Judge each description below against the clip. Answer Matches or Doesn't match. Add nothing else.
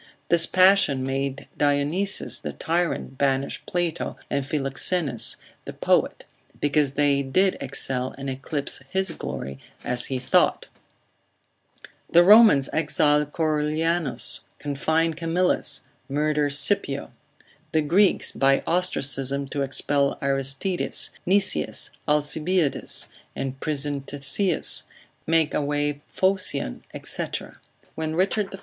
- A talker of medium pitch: Matches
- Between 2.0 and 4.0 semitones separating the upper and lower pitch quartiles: Matches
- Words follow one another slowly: Matches